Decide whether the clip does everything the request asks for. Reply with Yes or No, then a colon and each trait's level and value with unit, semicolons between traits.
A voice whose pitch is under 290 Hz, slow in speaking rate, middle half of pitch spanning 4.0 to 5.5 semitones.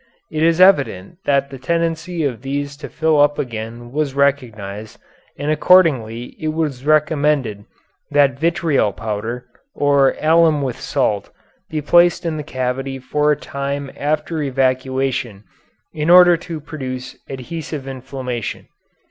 No: medium, 140 Hz; slow, 130 wpm; average, 3.4 semitones